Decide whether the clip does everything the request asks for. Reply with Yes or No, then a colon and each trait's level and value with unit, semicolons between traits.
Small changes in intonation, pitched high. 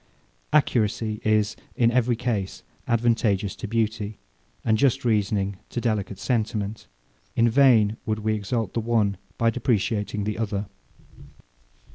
No: narrow, 2.1 semitones; low, 110 Hz